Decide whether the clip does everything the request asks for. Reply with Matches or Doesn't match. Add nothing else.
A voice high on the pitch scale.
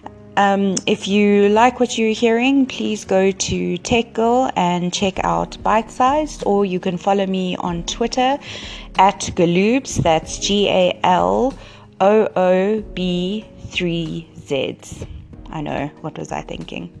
Matches